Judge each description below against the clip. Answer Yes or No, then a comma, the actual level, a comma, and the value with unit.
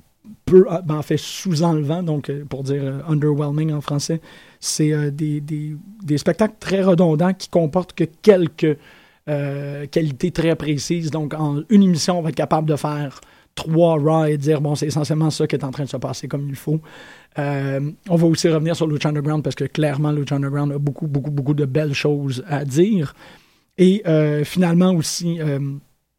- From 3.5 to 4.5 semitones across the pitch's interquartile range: No, narrow, 2.4 semitones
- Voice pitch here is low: No, medium, 155 Hz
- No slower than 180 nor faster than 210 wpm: Yes, average, 190 wpm